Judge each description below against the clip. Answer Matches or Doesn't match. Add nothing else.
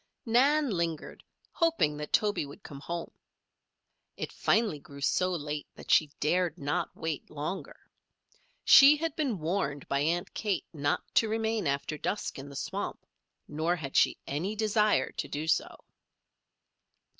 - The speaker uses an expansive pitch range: Matches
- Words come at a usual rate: Matches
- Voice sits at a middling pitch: Matches